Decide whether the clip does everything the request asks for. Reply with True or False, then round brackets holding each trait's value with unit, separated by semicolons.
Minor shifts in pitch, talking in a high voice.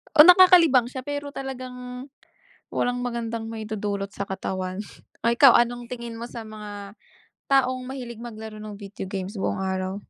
False (3.7 semitones; 235 Hz)